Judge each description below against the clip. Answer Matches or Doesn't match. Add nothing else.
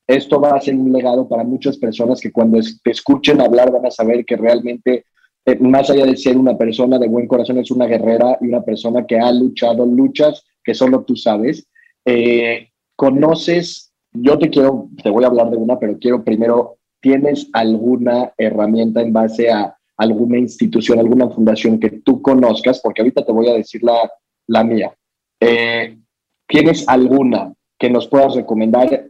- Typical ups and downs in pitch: Doesn't match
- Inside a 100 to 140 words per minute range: Doesn't match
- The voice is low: Matches